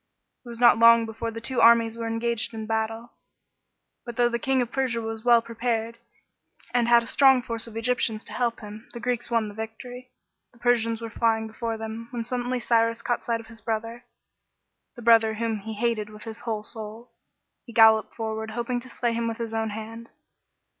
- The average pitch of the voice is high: Yes, high, 230 Hz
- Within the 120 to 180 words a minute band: No, average, 200 wpm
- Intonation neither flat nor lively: No, narrow, 1.2 semitones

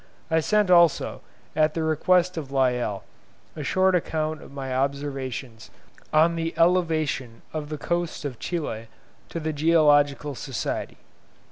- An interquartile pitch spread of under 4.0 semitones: Yes, average, 3.5 semitones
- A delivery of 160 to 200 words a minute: No, slow, 135 wpm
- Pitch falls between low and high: Yes, medium, 155 Hz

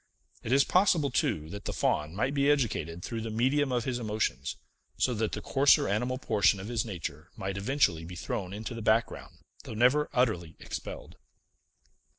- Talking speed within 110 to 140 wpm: No, average, 175 wpm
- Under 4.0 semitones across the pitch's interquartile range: No, average, 5.1 semitones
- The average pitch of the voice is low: Yes, low, 110 Hz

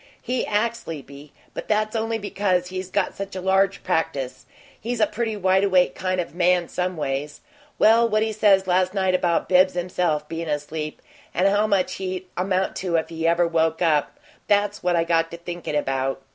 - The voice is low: No, medium, 185 Hz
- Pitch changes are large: No, average, 3.4 semitones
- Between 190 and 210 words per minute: Yes, average, 195 wpm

